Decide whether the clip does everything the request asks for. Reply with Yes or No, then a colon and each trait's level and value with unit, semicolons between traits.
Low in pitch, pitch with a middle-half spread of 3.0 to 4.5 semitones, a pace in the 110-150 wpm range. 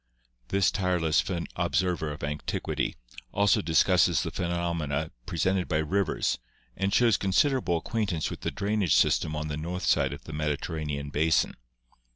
Yes: very low, 85 Hz; average, 3.7 semitones; average, 140 wpm